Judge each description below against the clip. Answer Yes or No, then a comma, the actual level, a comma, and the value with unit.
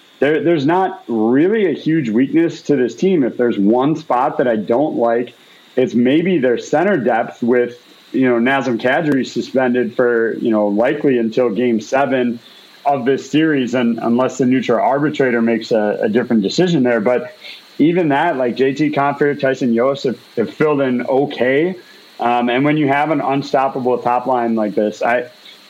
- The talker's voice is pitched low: Yes, low, 130 Hz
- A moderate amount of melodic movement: Yes, average, 3.0 semitones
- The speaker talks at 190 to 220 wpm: No, average, 175 wpm